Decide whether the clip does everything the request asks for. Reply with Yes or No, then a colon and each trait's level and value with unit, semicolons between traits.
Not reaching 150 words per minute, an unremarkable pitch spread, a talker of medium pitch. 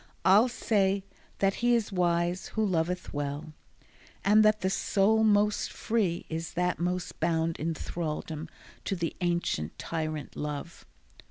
Yes: average, 140 wpm; average, 4.0 semitones; medium, 175 Hz